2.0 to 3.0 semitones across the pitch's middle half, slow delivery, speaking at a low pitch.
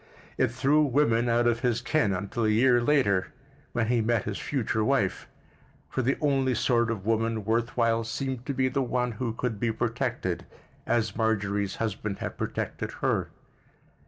No: narrow, 2.4 semitones; average, 170 wpm; low, 115 Hz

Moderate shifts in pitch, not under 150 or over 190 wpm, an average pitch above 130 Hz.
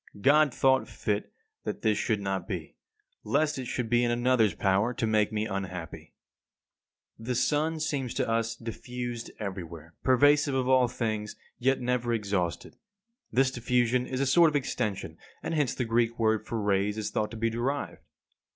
No: average, 3.5 semitones; average, 170 wpm; low, 120 Hz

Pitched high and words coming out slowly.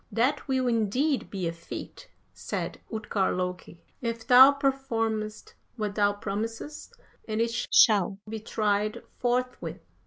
Yes: high, 225 Hz; slow, 125 wpm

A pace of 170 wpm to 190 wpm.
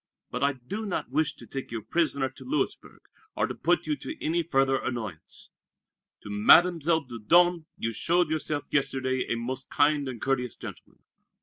Yes: average, 175 wpm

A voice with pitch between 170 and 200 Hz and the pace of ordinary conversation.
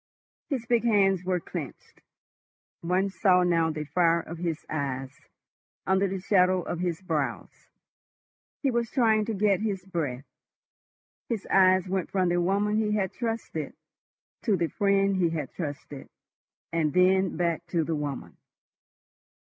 Yes: medium, 185 Hz; average, 145 wpm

